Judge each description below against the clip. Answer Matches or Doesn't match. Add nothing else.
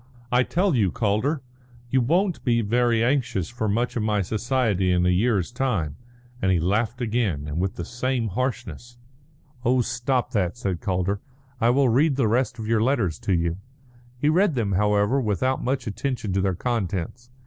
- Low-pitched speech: Matches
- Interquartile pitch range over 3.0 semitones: Matches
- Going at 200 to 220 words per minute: Doesn't match